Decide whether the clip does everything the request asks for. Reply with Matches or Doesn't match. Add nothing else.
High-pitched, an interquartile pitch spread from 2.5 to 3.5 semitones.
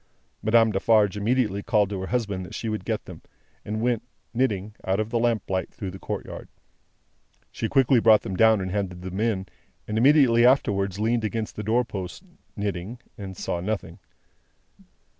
Doesn't match